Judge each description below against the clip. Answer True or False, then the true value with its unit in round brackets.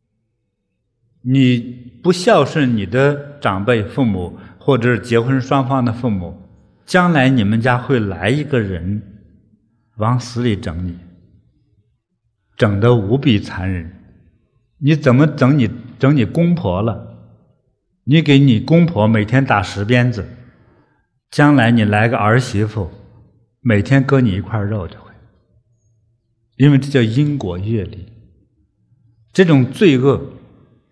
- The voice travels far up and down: False (4.1 semitones)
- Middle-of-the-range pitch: False (115 Hz)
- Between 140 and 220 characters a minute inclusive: True (175 characters per minute)